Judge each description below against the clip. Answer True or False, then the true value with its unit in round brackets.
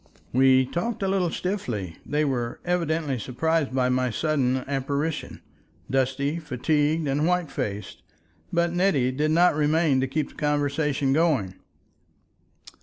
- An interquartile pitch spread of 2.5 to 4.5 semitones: True (3.7 semitones)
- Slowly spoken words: True (125 wpm)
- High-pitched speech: False (145 Hz)